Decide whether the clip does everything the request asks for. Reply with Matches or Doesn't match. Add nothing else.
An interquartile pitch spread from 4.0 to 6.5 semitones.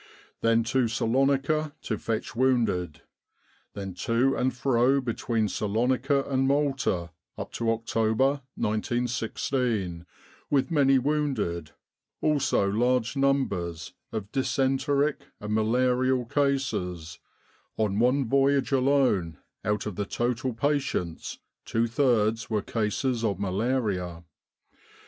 Matches